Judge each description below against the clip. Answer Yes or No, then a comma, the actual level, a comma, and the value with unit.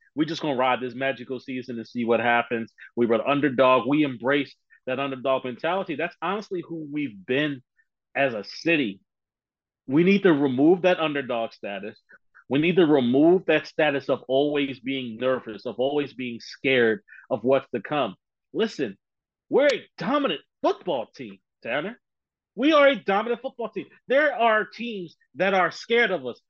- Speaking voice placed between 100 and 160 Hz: Yes, medium, 140 Hz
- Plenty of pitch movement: Yes, wide, 5.9 semitones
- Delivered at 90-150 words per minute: No, average, 165 wpm